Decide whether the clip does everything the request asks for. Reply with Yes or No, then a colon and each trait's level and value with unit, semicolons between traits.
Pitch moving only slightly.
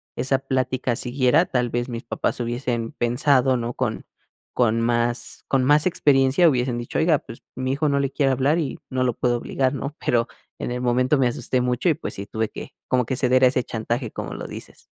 Yes: narrow, 2.0 semitones